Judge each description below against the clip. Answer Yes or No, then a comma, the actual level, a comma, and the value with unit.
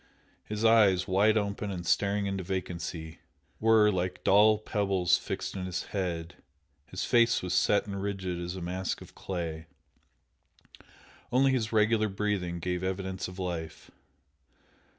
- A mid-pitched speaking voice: No, very low, 95 Hz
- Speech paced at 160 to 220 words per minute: No, average, 140 wpm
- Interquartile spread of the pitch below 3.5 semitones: Yes, average, 2.8 semitones